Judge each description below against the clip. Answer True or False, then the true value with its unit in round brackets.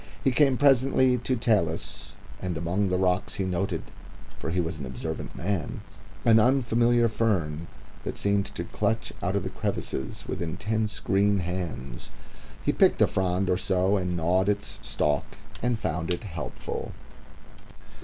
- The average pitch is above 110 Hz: False (95 Hz)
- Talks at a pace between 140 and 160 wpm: True (155 wpm)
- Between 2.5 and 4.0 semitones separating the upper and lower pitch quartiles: False (4.4 semitones)